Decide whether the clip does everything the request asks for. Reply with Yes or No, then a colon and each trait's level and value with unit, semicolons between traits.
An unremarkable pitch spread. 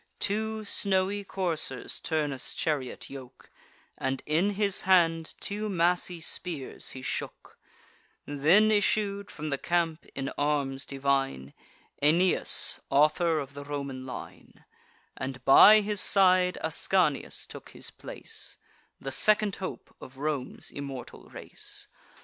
No: wide, 5.7 semitones